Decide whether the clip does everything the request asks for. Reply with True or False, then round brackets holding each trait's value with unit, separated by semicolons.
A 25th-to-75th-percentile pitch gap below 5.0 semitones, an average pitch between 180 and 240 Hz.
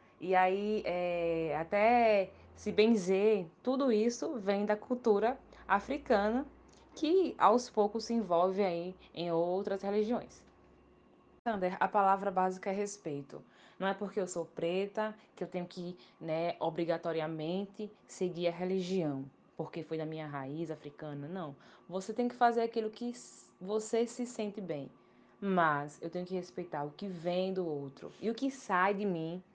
True (4.1 semitones; 190 Hz)